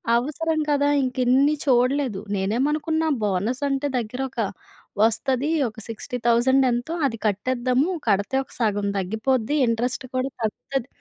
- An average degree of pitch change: Yes, average, 3.6 semitones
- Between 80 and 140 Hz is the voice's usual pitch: No, very high, 255 Hz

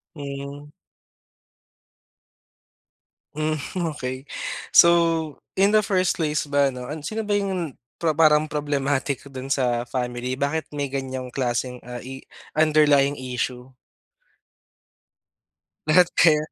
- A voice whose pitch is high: No, medium, 145 Hz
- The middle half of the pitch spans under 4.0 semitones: Yes, average, 3.2 semitones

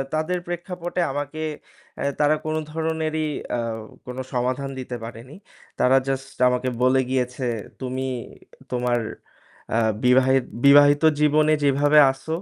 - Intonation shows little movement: No, average, 3.5 semitones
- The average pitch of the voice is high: No, low, 135 Hz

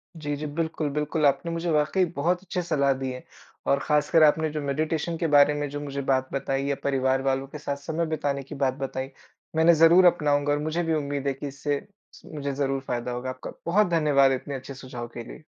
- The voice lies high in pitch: No, medium, 145 Hz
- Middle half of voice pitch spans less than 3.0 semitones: Yes, narrow, 2.6 semitones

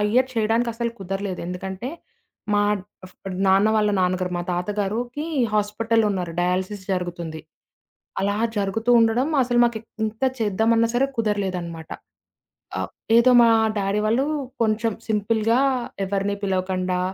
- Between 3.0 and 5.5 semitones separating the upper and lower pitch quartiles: Yes, average, 3.4 semitones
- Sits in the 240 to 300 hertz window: No, high, 205 Hz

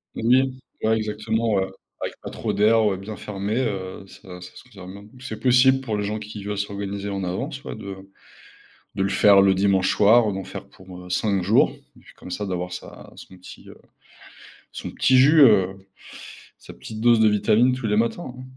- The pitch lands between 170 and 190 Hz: No, low, 105 Hz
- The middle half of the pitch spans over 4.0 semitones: No, average, 2.8 semitones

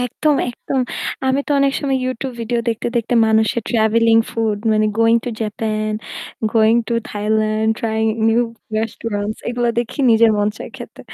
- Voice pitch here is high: Yes, high, 225 Hz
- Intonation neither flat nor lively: No, narrow, 1.6 semitones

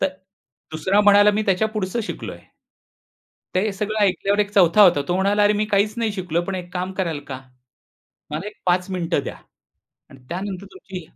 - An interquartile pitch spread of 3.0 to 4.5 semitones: No, narrow, 2.5 semitones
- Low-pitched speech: No, high, 195 Hz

